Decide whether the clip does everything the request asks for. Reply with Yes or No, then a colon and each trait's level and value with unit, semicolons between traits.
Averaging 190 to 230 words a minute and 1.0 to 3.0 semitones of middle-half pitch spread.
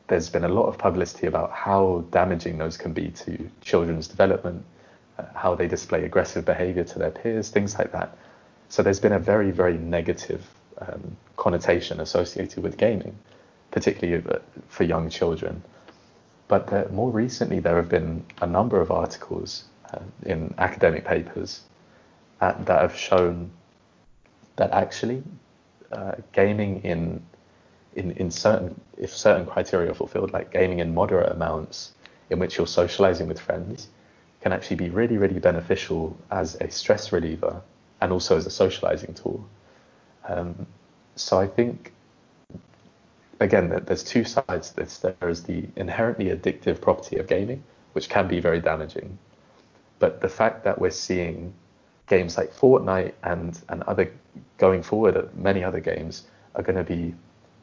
No: average, 155 wpm; narrow, 2.5 semitones